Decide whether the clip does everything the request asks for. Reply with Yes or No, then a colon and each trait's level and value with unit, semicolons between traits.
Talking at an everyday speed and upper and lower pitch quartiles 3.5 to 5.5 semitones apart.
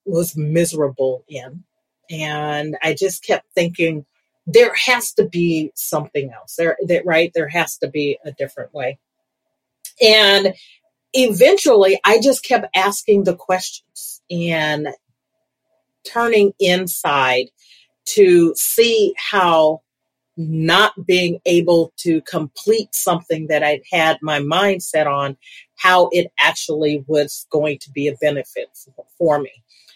No: slow, 125 wpm; average, 4.7 semitones